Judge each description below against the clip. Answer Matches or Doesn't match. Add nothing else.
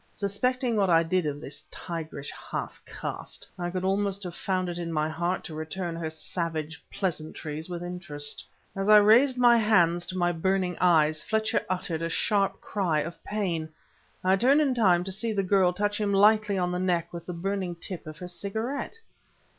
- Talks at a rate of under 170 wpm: Doesn't match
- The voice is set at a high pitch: Doesn't match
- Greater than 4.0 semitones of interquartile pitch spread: Doesn't match